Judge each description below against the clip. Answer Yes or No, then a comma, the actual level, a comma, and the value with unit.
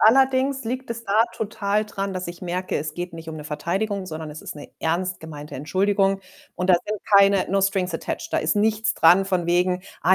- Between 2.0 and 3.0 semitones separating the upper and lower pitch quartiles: No, average, 3.5 semitones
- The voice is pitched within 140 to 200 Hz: Yes, medium, 185 Hz